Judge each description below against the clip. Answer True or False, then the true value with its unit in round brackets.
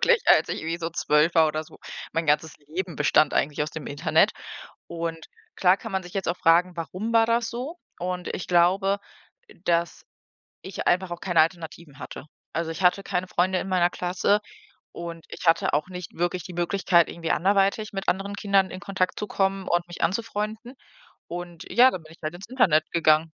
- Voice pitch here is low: False (175 Hz)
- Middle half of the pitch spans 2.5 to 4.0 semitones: True (2.8 semitones)